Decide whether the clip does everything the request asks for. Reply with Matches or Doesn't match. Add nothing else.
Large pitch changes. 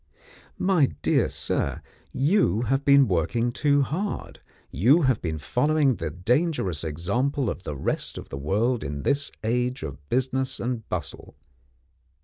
Matches